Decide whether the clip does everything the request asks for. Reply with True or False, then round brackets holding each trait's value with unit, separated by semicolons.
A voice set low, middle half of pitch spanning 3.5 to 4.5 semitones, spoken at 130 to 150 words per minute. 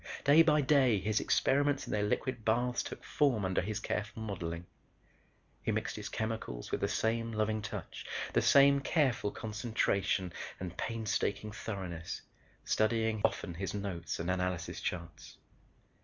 True (110 Hz; 4.0 semitones; 140 wpm)